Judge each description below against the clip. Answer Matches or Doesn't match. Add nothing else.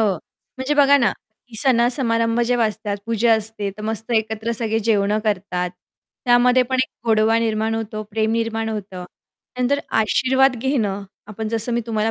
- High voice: Matches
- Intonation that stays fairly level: Matches